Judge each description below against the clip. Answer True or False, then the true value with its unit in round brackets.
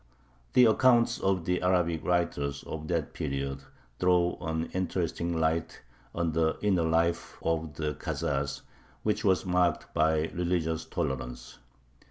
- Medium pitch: False (85 Hz)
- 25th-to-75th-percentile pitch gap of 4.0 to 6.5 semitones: False (2.5 semitones)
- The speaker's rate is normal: False (130 wpm)